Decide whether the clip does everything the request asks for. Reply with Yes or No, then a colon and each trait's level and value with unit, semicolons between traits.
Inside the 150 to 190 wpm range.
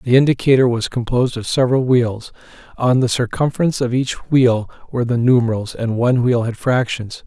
Yes: average, 175 wpm